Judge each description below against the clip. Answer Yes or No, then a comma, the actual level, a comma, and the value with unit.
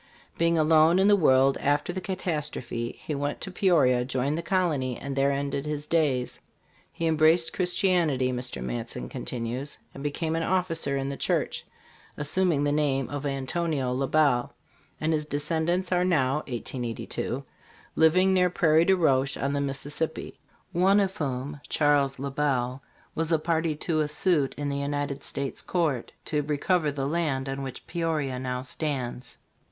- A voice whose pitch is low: No, medium, 145 Hz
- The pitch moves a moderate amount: Yes, average, 3.4 semitones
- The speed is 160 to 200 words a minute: Yes, average, 165 wpm